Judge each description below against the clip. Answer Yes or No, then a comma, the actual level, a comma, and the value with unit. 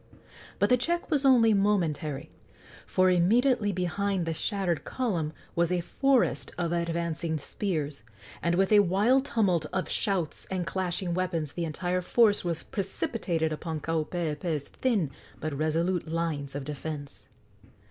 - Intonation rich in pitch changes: No, average, 4.1 semitones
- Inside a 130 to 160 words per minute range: Yes, slow, 135 wpm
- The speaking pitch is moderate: Yes, medium, 175 Hz